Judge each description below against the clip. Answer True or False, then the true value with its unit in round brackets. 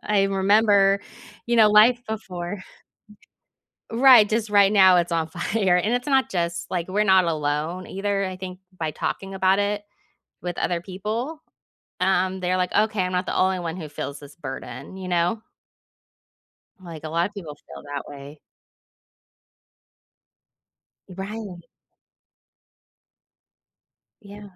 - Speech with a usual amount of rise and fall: True (3.1 semitones)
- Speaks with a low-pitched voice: False (190 Hz)